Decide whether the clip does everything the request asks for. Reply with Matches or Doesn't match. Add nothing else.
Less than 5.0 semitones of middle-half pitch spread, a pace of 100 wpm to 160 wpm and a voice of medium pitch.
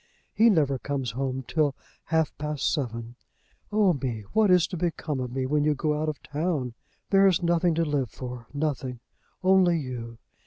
Doesn't match